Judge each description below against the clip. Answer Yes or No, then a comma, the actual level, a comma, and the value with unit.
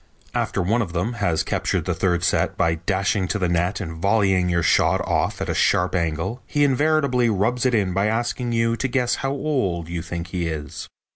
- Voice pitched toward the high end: No, very low, 95 Hz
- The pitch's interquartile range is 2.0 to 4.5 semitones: No, wide, 5.6 semitones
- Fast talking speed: Yes, fast, 210 wpm